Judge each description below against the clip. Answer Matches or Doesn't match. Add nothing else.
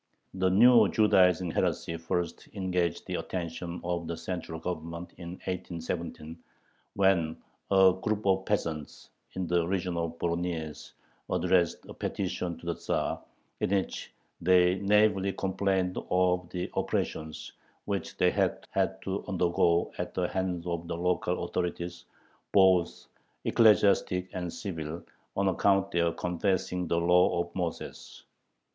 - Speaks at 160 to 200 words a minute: Doesn't match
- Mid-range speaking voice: Doesn't match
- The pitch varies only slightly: Matches